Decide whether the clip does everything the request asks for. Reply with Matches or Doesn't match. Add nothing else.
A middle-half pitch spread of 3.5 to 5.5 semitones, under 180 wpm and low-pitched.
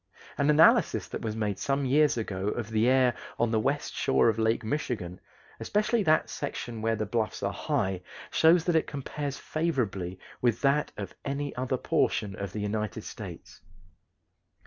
Matches